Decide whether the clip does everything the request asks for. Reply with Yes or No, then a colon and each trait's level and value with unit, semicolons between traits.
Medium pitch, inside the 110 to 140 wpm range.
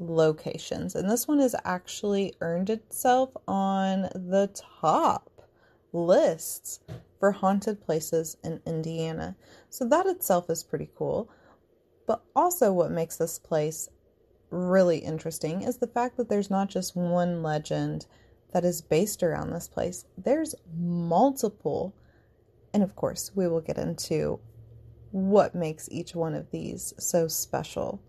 Yes: medium, 180 Hz; slow, 135 wpm